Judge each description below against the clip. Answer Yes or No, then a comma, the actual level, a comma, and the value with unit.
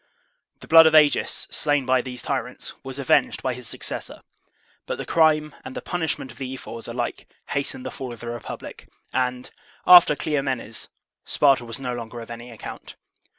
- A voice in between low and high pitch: No, low, 130 Hz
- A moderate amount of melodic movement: Yes, average, 3.7 semitones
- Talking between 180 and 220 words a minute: Yes, average, 185 wpm